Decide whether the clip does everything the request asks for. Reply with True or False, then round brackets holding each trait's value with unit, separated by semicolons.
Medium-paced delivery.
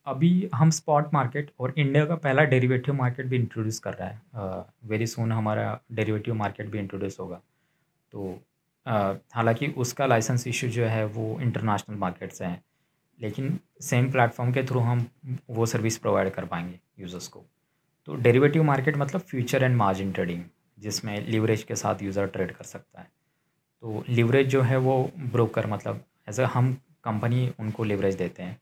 True (170 wpm)